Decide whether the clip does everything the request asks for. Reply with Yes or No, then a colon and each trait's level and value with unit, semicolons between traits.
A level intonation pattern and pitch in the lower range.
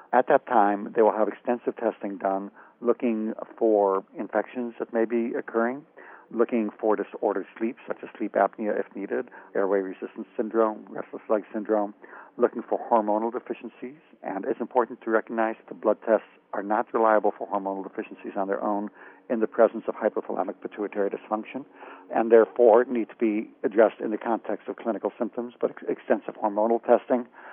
Yes: narrow, 2.3 semitones; low, 110 Hz